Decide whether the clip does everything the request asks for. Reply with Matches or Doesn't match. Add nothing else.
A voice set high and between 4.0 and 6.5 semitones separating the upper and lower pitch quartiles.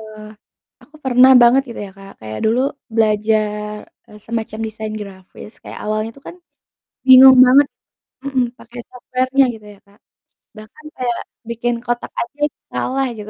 Doesn't match